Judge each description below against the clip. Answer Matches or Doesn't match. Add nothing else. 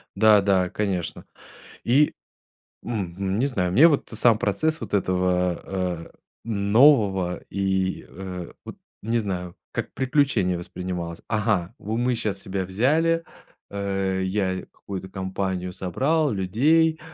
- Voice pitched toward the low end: Matches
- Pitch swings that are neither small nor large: Matches